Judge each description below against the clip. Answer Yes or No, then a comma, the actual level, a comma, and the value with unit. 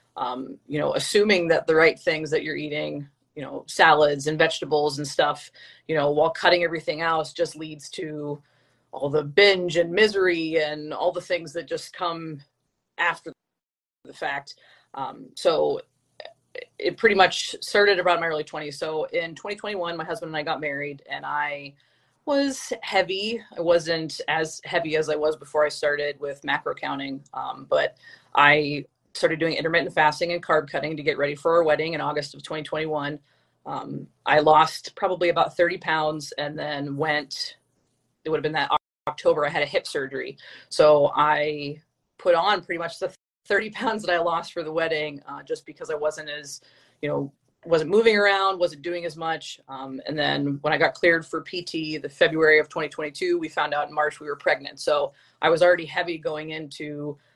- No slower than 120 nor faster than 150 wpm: No, average, 185 wpm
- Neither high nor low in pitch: Yes, medium, 160 Hz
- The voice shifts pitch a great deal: No, average, 2.8 semitones